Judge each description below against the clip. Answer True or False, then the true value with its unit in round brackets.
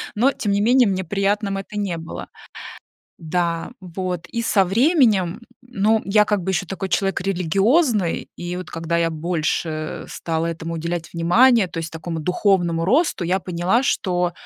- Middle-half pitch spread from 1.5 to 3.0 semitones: False (3.7 semitones)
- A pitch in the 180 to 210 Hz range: True (185 Hz)